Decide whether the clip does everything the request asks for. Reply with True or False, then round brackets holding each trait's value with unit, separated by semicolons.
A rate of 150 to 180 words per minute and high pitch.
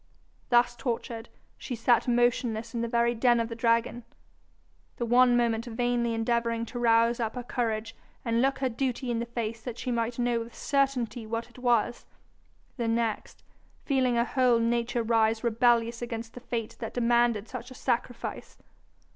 True (170 wpm; 235 Hz)